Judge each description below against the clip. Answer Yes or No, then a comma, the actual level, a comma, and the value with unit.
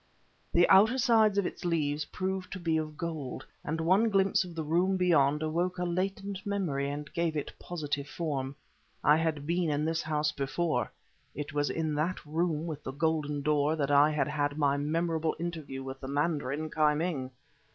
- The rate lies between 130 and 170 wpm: No, average, 185 wpm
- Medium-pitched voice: Yes, medium, 155 Hz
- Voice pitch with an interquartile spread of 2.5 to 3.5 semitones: Yes, average, 3.0 semitones